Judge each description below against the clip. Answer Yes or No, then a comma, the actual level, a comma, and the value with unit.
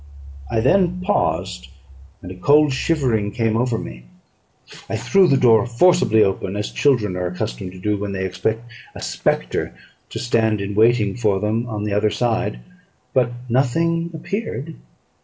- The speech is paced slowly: No, average, 160 wpm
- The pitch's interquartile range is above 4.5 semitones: Yes, average, 5.0 semitones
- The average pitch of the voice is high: No, low, 110 Hz